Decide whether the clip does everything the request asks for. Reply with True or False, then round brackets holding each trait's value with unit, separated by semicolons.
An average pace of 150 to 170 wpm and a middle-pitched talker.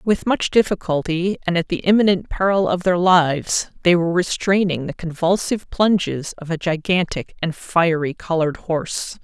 True (155 wpm; 175 Hz)